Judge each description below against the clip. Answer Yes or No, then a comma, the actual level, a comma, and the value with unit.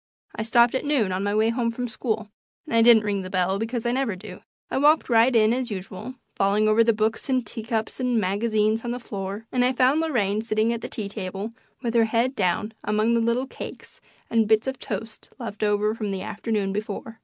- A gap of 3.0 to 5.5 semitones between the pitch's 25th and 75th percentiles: No, narrow, 2.4 semitones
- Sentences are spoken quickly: Yes, fast, 225 wpm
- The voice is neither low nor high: No, high, 225 Hz